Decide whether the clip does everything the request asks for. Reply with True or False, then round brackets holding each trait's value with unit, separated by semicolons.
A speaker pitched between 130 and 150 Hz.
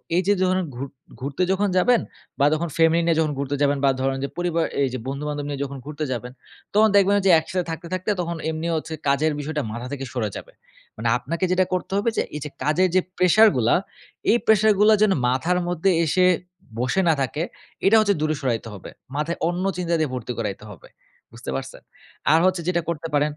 False (160 Hz)